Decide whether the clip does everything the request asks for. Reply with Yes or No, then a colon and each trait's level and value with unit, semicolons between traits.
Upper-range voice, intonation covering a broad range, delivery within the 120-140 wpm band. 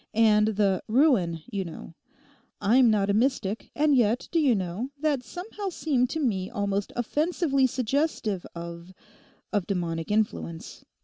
Yes: high, 215 Hz; wide, 6.0 semitones; slow, 135 wpm